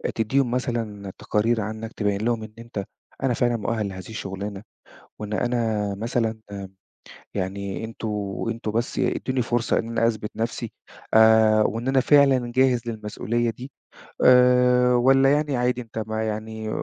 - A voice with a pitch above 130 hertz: No, low, 115 Hz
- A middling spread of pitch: No, narrow, 2.3 semitones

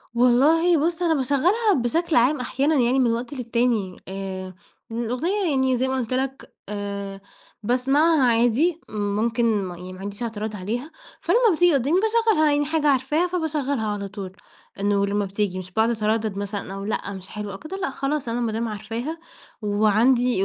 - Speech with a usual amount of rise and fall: No, wide, 6.1 semitones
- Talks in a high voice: Yes, high, 240 Hz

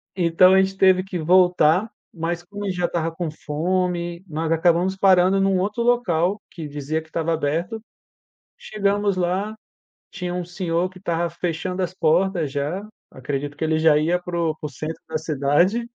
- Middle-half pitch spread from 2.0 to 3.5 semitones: Yes, average, 2.8 semitones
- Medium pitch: Yes, medium, 175 Hz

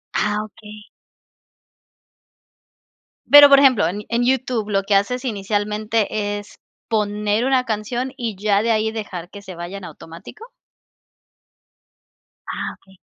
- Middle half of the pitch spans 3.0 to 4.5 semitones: No, narrow, 2.5 semitones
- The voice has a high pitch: Yes, high, 210 Hz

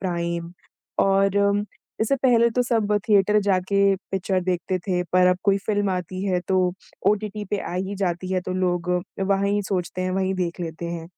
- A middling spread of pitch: No, narrow, 2.0 semitones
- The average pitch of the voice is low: No, high, 190 Hz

